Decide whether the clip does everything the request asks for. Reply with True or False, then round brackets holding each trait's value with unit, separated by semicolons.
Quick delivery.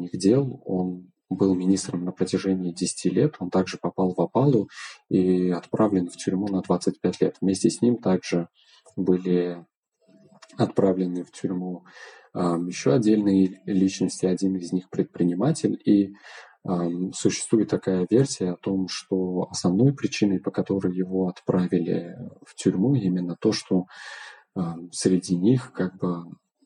False (135 wpm)